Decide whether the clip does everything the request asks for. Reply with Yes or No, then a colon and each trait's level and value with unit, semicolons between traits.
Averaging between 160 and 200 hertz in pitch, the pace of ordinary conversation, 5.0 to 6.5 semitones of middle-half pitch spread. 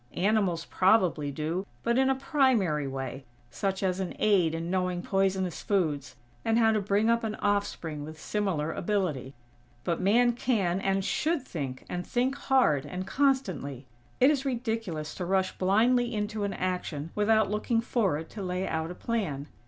Yes: high, 190 Hz; average, 165 wpm; wide, 5.4 semitones